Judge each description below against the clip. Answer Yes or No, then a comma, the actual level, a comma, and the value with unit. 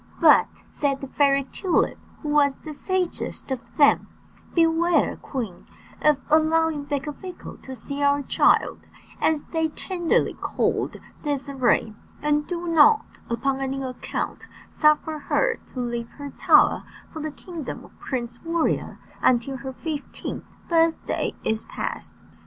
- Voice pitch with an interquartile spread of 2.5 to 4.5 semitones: Yes, average, 3.3 semitones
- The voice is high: Yes, very high, 290 Hz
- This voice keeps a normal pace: No, slow, 130 wpm